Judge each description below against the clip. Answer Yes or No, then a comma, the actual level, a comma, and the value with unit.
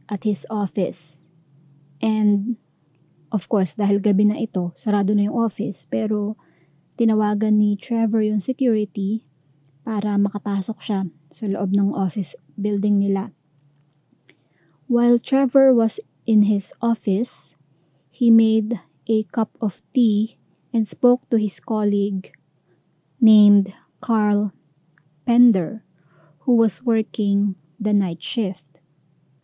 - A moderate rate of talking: No, slow, 110 wpm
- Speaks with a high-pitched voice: Yes, high, 205 Hz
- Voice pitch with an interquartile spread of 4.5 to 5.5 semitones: Yes, average, 5.2 semitones